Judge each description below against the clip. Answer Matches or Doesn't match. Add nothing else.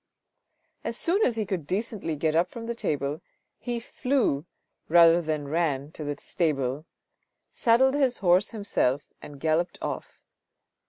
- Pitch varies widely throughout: Matches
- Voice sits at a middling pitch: Matches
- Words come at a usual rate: Matches